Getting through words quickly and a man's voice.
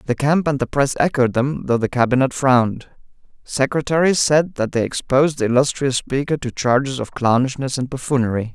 No: average, 170 wpm; male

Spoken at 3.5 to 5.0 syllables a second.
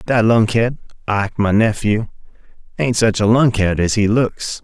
Yes: 4.5 syllables/s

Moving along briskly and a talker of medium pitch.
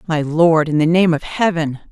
Yes: fast, 220 wpm; medium, 160 Hz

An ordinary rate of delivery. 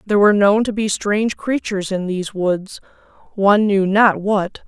Yes: average, 180 wpm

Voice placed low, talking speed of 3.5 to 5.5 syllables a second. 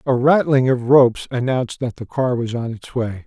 Yes: low, 125 Hz; 5.2 syllables/s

